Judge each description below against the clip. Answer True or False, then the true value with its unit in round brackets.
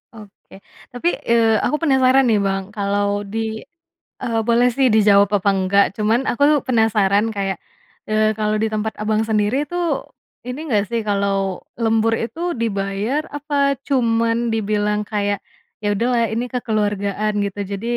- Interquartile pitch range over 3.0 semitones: False (2.4 semitones)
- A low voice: False (215 Hz)